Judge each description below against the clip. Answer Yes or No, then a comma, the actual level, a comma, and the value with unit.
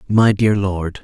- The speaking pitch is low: Yes, low, 100 Hz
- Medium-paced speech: Yes, average, 175 wpm